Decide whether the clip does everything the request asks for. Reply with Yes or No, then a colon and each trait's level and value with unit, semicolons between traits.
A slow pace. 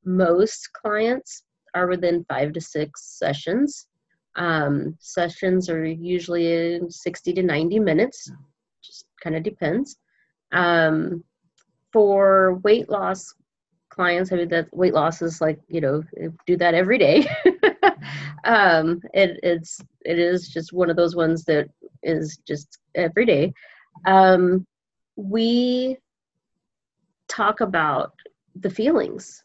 Yes: slow, 120 wpm